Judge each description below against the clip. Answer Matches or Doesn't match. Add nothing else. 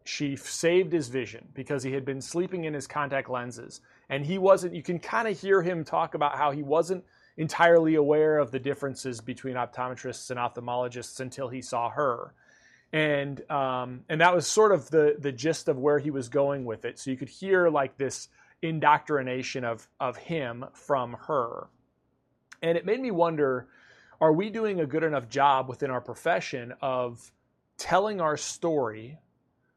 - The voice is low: Doesn't match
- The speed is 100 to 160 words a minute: Doesn't match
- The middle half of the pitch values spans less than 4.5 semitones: Matches